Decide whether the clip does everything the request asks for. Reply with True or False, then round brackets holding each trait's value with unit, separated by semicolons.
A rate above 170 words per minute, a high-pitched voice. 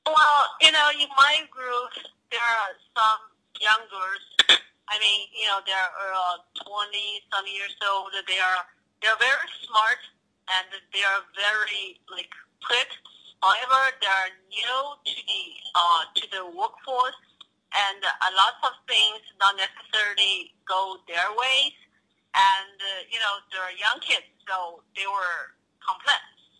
False (140 wpm; 205 Hz)